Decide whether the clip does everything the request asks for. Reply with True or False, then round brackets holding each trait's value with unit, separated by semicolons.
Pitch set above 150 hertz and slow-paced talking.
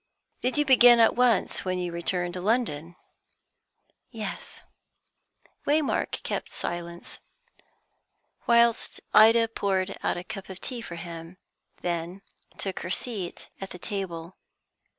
True (190 Hz; 130 wpm)